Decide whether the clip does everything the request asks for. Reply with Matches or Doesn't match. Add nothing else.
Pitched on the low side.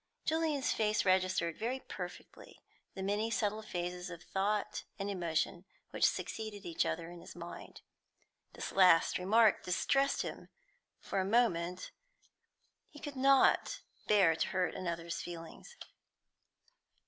Doesn't match